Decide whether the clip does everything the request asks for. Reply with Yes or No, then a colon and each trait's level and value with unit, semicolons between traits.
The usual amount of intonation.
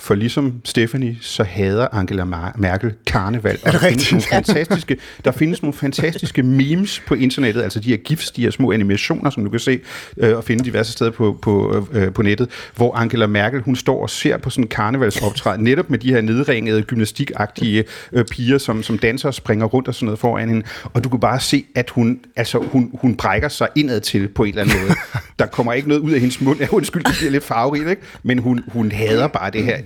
Yes: average, 3.7 semitones